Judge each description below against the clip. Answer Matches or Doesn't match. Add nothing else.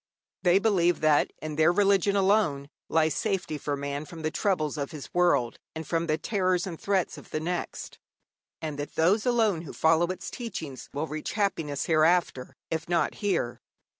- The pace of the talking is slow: Doesn't match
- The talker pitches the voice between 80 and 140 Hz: Doesn't match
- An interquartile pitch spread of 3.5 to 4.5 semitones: Matches